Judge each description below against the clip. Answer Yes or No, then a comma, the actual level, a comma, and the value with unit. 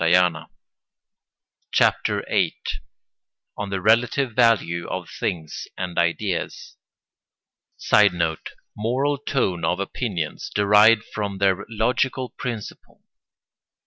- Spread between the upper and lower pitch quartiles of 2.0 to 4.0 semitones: No, average, 4.5 semitones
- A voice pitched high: No, low, 105 Hz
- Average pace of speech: No, slow, 85 wpm